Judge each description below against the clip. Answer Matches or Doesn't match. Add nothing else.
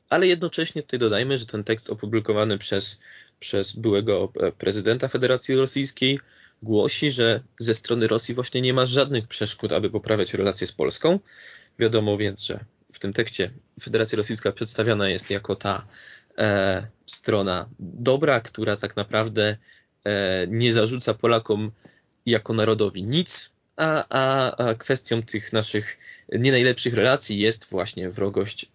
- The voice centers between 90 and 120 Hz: Matches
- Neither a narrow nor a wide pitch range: Matches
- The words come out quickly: Doesn't match